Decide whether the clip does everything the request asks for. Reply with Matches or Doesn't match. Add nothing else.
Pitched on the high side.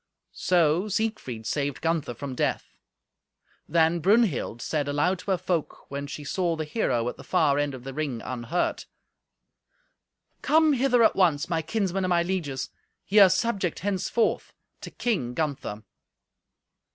Doesn't match